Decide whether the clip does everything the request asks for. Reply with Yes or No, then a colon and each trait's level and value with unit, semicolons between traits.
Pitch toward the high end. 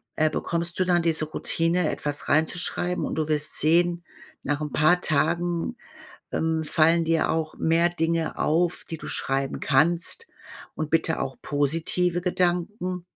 No: medium, 165 Hz